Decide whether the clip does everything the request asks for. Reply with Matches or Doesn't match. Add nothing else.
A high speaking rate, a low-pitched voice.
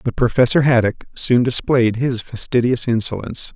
Doesn't match